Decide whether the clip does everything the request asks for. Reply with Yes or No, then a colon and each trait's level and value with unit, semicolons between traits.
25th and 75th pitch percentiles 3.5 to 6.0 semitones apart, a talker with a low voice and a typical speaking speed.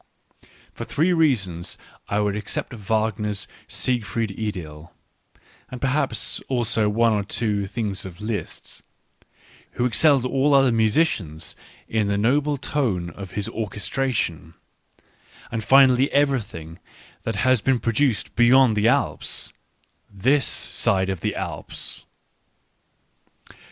No: average, 4.6 semitones; low, 110 Hz; slow, 120 wpm